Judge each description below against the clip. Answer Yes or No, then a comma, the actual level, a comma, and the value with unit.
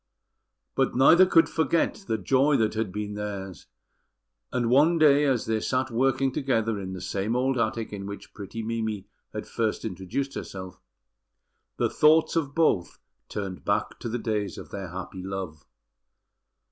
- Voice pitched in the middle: No, low, 110 Hz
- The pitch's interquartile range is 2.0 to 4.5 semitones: No, wide, 5.4 semitones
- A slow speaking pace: No, average, 160 wpm